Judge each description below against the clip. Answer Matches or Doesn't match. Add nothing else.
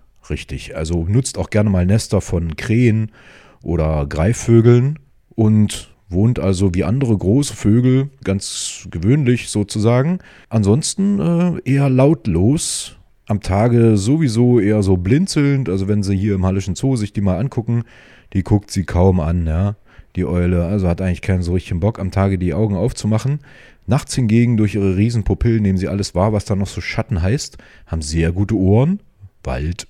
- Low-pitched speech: Matches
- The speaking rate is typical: Matches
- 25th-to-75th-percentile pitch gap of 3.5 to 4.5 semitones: Matches